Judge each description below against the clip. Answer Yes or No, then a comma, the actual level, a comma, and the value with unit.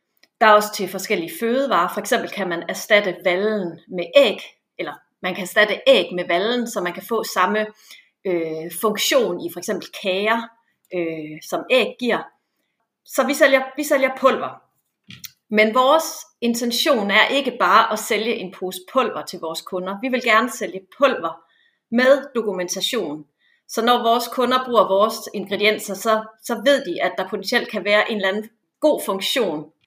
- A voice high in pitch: Yes, high, 215 Hz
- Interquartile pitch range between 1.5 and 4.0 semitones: No, average, 4.8 semitones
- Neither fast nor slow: Yes, average, 170 wpm